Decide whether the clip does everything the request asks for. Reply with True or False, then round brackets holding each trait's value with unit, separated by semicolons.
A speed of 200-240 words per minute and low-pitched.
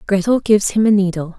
False (215 wpm; 200 Hz)